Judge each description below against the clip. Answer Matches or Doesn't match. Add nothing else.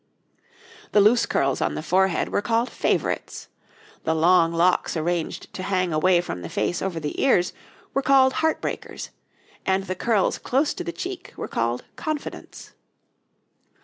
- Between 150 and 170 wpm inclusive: Matches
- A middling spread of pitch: Doesn't match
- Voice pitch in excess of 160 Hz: Matches